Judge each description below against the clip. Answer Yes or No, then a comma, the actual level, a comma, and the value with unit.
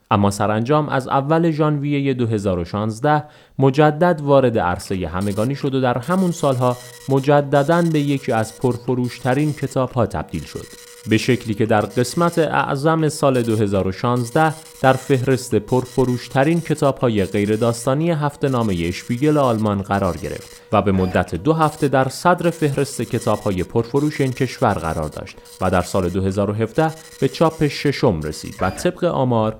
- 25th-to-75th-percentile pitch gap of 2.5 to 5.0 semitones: No, wide, 5.4 semitones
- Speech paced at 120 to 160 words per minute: Yes, average, 145 wpm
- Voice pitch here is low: Yes, low, 130 Hz